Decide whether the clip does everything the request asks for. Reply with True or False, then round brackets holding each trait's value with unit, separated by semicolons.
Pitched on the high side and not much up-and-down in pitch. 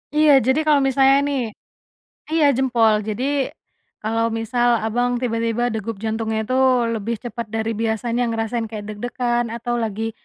True (235 Hz; 2.2 semitones)